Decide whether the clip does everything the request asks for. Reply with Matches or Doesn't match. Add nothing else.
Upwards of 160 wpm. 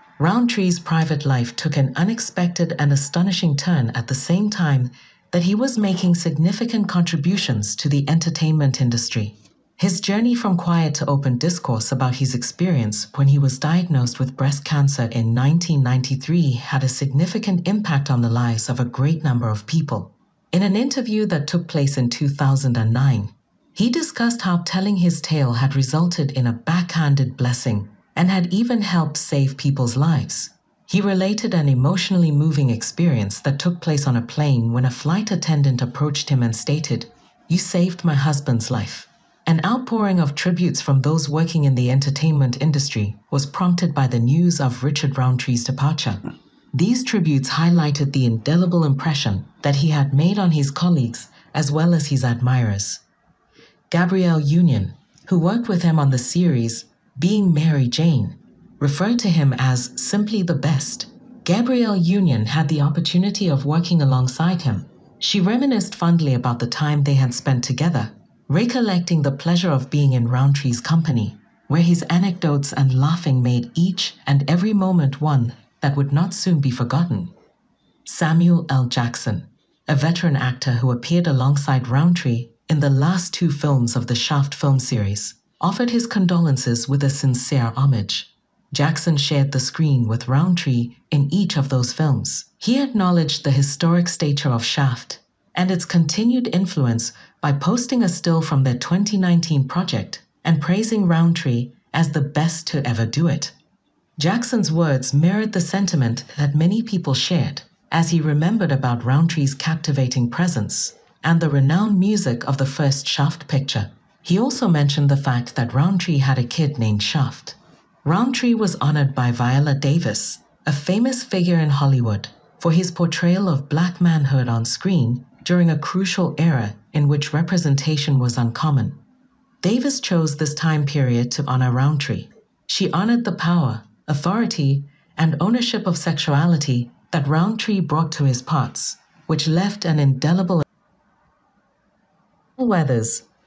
Doesn't match